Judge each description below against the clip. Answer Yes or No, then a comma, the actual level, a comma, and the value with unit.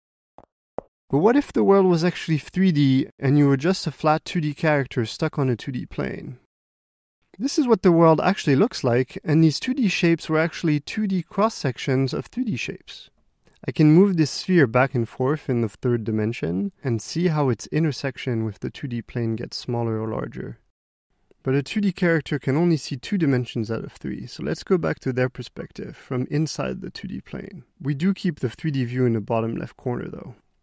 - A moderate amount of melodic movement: No, wide, 5.8 semitones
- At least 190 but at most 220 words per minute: Yes, average, 200 wpm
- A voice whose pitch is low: No, medium, 150 Hz